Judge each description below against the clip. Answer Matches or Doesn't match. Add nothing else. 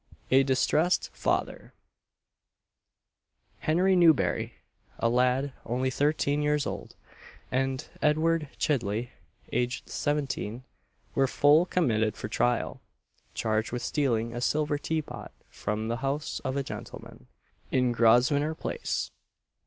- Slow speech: Matches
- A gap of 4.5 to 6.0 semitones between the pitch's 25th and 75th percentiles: Doesn't match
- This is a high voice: Doesn't match